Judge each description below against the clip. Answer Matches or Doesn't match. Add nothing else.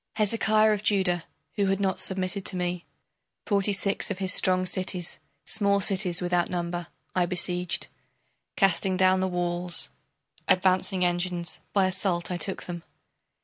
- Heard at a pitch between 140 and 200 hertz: Matches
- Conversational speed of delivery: Matches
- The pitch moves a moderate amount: Doesn't match